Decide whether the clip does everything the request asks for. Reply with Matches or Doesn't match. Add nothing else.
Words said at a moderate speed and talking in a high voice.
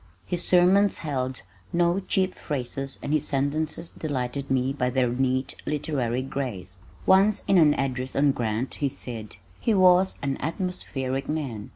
Doesn't match